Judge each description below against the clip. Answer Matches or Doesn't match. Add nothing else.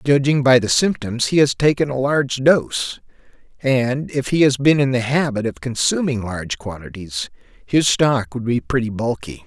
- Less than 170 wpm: Doesn't match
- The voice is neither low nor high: Doesn't match